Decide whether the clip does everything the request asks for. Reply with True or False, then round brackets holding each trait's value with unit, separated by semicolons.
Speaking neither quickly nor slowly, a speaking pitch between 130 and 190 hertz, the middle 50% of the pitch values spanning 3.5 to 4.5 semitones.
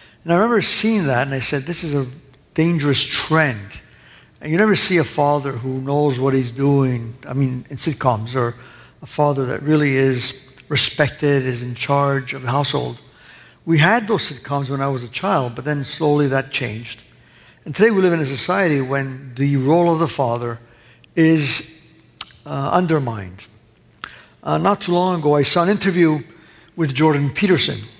True (180 wpm; 140 Hz; 4.0 semitones)